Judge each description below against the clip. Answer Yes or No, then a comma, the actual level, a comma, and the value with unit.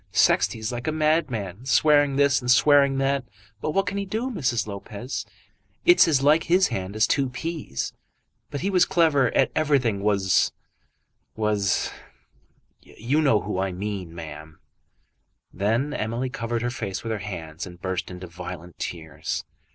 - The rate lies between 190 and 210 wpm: No, average, 160 wpm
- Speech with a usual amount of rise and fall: No, wide, 7.1 semitones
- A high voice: No, low, 120 Hz